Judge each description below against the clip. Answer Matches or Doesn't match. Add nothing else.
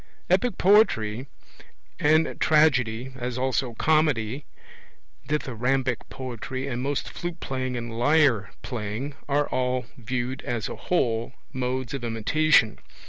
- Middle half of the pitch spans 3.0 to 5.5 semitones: Matches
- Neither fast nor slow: Doesn't match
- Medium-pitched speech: Doesn't match